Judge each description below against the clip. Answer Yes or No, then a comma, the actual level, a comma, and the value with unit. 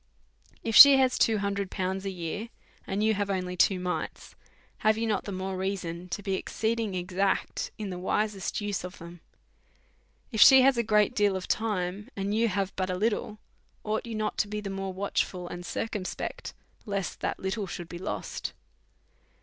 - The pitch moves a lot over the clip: No, narrow, 2.5 semitones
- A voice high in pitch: Yes, high, 200 Hz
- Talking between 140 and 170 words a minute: No, average, 180 wpm